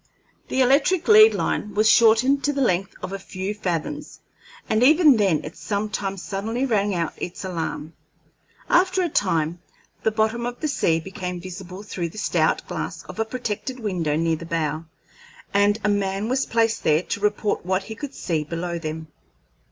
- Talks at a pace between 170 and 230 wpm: Yes, average, 175 wpm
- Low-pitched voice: No, high, 205 Hz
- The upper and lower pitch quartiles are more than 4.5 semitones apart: Yes, average, 5.1 semitones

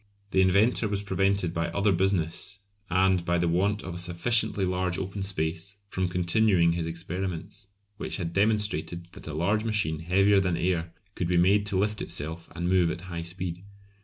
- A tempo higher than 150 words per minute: Yes, average, 180 wpm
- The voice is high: No, very low, 90 Hz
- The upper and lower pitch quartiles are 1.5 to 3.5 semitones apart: Yes, narrow, 2.6 semitones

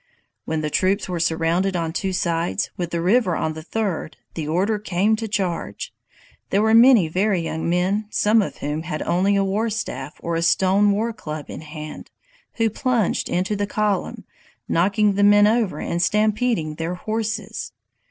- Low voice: No, high, 190 Hz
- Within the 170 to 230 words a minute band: Yes, average, 175 wpm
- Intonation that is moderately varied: Yes, average, 4.1 semitones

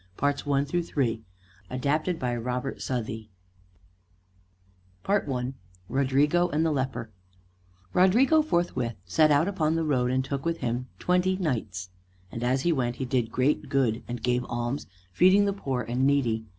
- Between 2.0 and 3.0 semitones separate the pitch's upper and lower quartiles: No, average, 4.7 semitones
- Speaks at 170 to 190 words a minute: No, average, 155 wpm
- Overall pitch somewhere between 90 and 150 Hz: Yes, low, 135 Hz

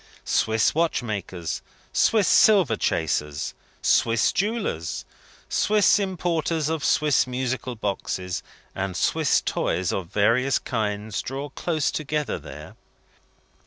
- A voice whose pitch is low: Yes, low, 125 Hz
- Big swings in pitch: Yes, wide, 7.8 semitones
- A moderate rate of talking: No, slow, 100 wpm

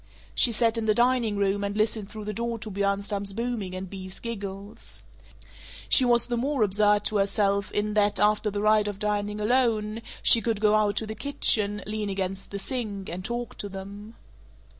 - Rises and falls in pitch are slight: Yes, narrow, 2.0 semitones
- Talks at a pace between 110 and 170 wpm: No, average, 190 wpm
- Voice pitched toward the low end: No, high, 210 Hz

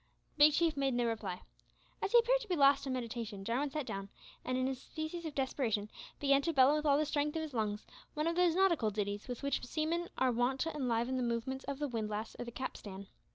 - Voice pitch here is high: Yes, very high, 265 Hz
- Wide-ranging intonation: No, average, 4.7 semitones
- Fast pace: Yes, fast, 235 wpm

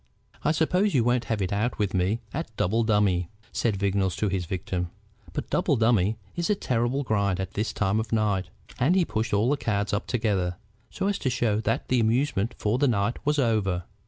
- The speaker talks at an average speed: No, fast, 210 wpm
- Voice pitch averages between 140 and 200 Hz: No, low, 110 Hz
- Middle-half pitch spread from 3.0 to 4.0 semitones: Yes, average, 3.7 semitones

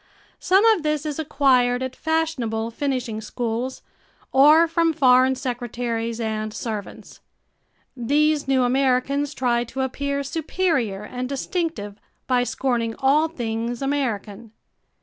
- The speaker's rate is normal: No, slow, 115 wpm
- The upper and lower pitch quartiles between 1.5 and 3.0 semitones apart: No, average, 3.7 semitones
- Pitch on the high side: Yes, very high, 260 Hz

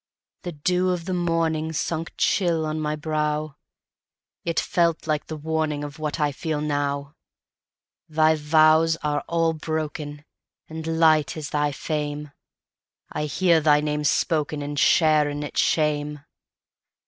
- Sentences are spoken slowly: Yes, slow, 115 wpm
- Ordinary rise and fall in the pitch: No, narrow, 1.5 semitones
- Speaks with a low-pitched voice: No, medium, 155 Hz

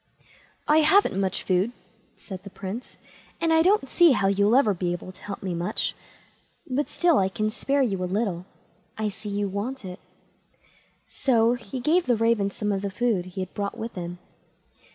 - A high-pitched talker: Yes, high, 210 Hz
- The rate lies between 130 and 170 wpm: No, average, 190 wpm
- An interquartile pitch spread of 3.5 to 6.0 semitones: Yes, average, 4.8 semitones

